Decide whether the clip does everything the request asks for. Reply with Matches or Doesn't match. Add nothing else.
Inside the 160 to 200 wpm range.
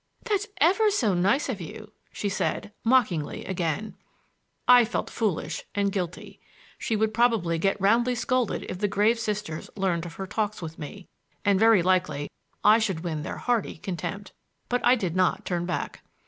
Matches